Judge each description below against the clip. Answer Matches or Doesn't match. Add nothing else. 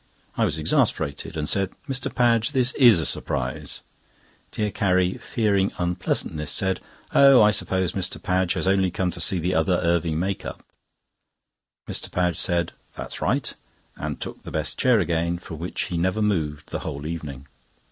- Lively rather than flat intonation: Doesn't match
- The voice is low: Matches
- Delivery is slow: Doesn't match